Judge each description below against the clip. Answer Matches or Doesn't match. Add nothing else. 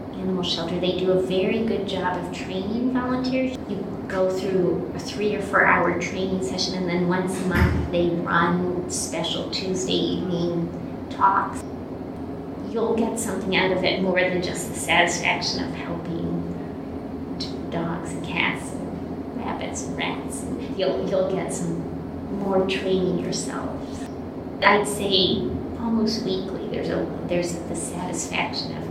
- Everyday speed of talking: Matches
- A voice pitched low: Doesn't match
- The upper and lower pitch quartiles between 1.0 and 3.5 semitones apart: Matches